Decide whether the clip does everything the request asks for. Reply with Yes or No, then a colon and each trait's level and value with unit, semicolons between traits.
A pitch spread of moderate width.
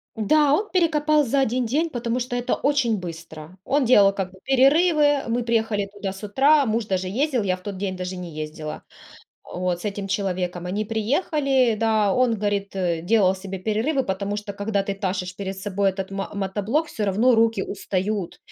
Yes: average, 4.8 semitones